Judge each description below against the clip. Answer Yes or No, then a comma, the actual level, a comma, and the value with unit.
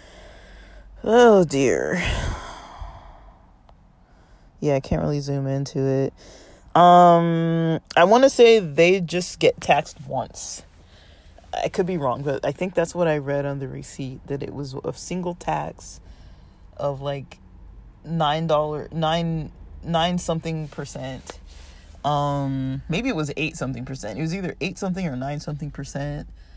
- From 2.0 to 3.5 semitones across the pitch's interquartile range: No, average, 3.9 semitones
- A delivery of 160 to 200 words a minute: No, average, 140 wpm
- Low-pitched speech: No, medium, 145 Hz